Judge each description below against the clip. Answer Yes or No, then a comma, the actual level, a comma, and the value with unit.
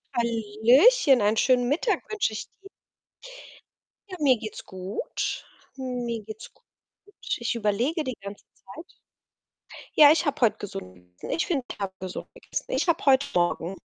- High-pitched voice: Yes, high, 240 Hz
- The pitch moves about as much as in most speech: No, wide, 5.7 semitones